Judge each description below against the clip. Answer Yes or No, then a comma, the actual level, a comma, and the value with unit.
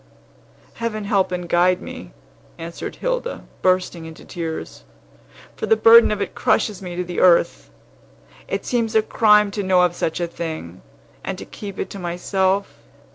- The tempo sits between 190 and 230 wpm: No, average, 165 wpm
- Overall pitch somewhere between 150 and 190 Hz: Yes, medium, 185 Hz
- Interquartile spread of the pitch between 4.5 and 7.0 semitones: No, average, 3.4 semitones